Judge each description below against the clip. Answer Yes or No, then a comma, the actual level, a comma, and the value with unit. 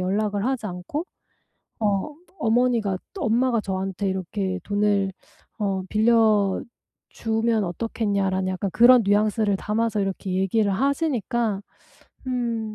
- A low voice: No, high, 210 Hz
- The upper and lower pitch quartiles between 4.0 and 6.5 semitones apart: No, average, 3.0 semitones